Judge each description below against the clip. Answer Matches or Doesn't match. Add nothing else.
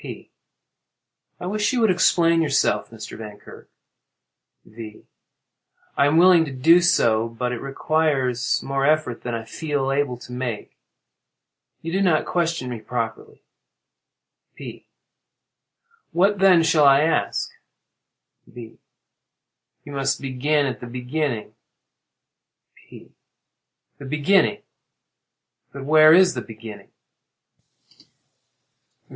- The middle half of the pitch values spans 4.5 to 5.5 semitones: Matches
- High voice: Doesn't match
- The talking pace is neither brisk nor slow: Doesn't match